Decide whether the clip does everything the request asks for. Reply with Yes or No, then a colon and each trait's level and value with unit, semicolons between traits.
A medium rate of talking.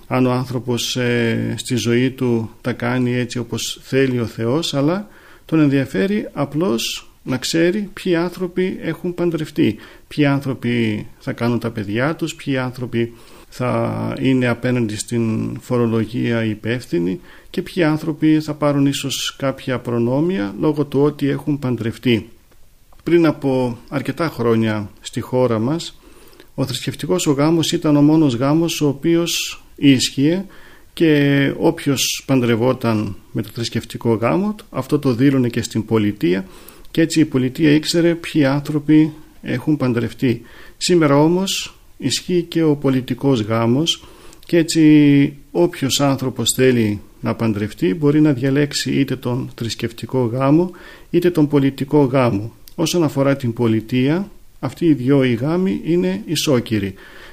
Yes: average, 135 wpm